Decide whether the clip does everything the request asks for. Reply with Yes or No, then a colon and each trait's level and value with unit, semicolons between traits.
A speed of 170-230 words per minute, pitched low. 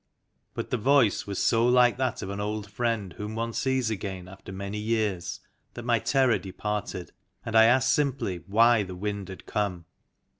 Yes: average, 180 wpm; low, 105 Hz